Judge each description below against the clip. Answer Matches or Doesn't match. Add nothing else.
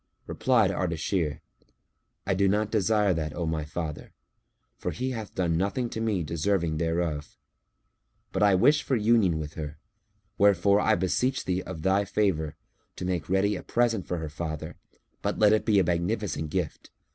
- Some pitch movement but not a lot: Matches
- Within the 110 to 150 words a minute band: Doesn't match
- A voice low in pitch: Matches